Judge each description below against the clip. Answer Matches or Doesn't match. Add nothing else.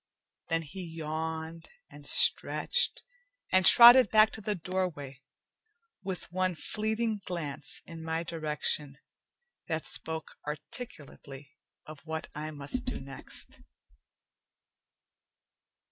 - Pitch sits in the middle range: Matches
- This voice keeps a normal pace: Doesn't match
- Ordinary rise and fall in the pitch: Matches